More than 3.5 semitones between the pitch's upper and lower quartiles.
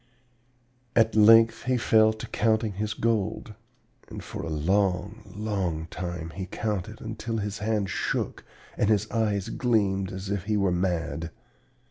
No: average, 2.7 semitones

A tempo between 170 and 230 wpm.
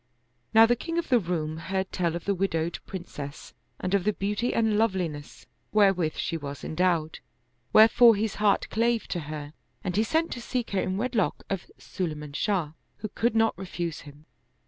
Yes: average, 180 wpm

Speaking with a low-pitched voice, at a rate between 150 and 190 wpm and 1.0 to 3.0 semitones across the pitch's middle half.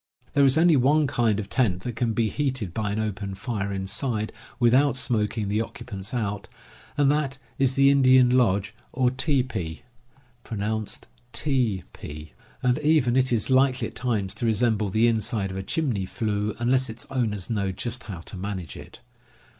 No: low, 115 Hz; average, 180 wpm; average, 4.3 semitones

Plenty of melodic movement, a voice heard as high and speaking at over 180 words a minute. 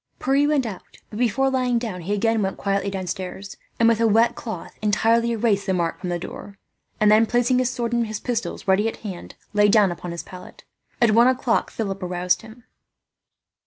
No: average, 3.4 semitones; high, 215 Hz; average, 200 wpm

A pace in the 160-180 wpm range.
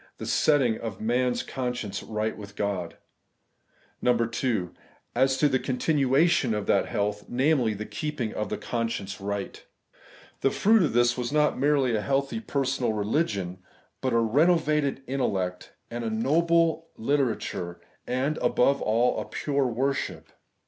No: average, 150 wpm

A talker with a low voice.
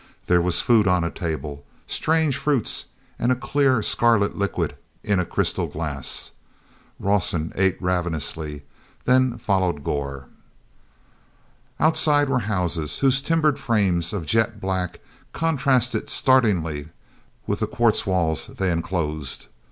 Yes: very low, 95 Hz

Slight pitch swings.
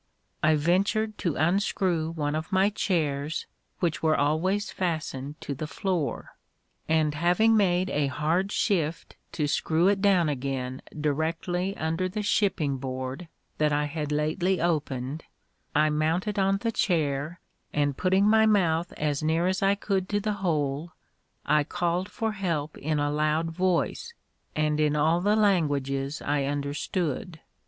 No: average, 4.2 semitones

